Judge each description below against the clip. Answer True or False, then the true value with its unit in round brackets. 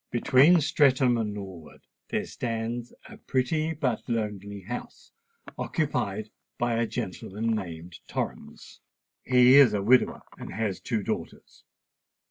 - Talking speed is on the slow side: True (120 wpm)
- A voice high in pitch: False (115 Hz)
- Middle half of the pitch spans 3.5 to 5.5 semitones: True (3.8 semitones)